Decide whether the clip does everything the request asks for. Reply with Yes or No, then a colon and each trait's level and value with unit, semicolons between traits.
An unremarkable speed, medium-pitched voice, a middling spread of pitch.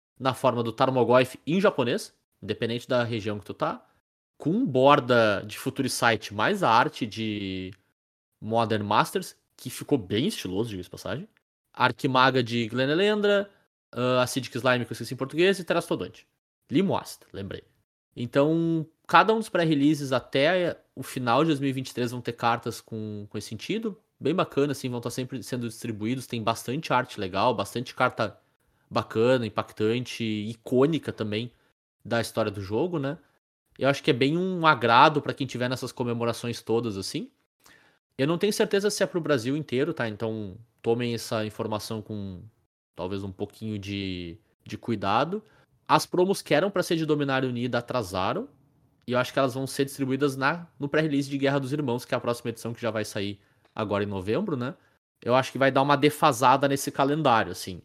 No: average, 175 wpm; low, 125 Hz; average, 4.0 semitones